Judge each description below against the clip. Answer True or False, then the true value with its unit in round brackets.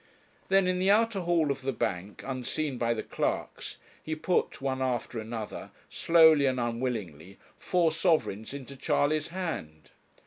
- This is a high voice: False (135 Hz)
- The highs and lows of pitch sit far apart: True (6.0 semitones)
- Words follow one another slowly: False (145 wpm)